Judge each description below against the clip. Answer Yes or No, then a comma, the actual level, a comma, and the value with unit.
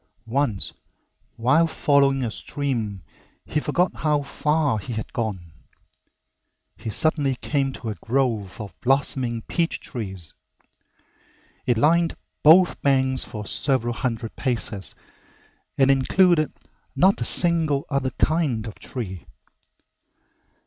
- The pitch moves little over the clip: No, average, 4.8 semitones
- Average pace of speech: No, slow, 115 wpm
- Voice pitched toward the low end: Yes, low, 130 Hz